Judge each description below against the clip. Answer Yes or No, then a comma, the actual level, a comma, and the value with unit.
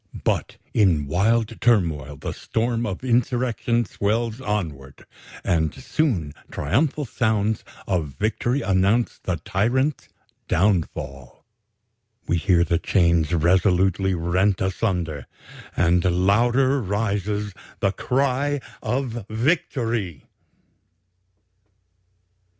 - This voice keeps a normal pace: No, slow, 90 wpm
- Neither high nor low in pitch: No, low, 100 Hz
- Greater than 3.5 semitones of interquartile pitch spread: Yes, wide, 5.4 semitones